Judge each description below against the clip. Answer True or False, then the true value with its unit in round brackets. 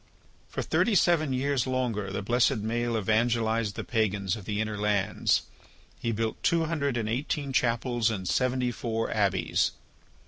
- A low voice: True (115 Hz)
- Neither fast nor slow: True (150 wpm)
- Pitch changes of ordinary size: True (3.2 semitones)